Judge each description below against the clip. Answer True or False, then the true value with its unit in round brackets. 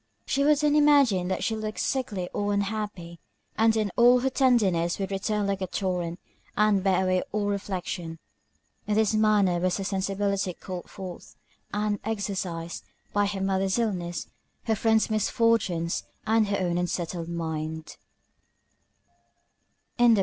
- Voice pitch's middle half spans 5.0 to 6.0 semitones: False (3.2 semitones)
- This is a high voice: True (200 Hz)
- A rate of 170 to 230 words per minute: False (140 wpm)